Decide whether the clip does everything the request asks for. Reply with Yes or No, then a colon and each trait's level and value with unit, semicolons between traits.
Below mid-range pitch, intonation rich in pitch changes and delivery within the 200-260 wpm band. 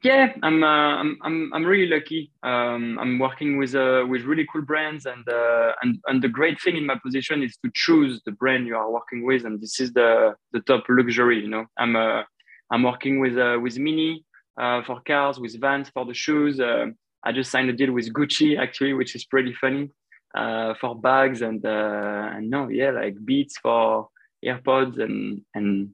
No: low, 130 Hz; average, 3.8 semitones; fast, 205 wpm